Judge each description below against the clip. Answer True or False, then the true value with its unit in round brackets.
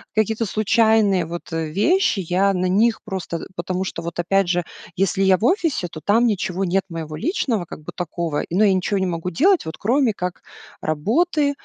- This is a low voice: False (190 Hz)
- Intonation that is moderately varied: True (4.2 semitones)